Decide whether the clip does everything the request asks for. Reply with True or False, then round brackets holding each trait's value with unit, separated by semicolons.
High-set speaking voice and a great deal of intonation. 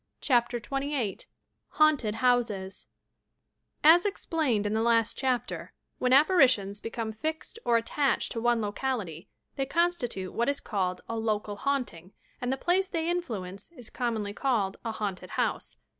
False (240 Hz; 5.0 semitones)